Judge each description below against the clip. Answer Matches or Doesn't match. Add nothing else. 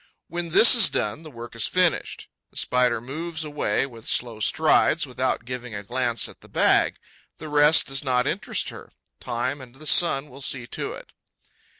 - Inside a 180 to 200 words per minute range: Matches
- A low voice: Matches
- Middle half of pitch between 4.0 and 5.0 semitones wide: Matches